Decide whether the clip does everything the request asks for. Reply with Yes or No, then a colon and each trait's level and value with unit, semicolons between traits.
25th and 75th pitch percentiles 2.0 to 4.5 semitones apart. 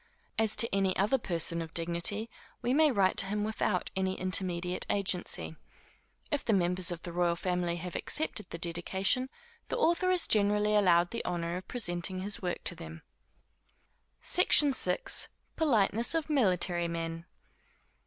Yes: average, 4.0 semitones